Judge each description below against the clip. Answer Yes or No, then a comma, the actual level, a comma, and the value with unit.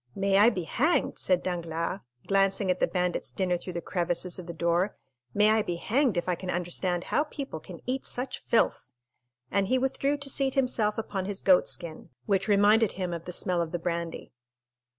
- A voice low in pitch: No, medium, 185 Hz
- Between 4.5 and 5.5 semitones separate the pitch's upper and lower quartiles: No, average, 3.8 semitones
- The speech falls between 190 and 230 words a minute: Yes, average, 195 wpm